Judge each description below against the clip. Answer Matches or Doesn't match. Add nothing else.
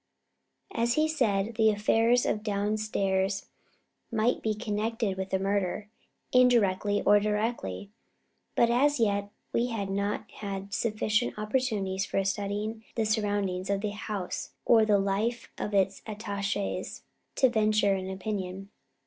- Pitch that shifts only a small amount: Matches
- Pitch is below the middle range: Doesn't match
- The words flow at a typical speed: Doesn't match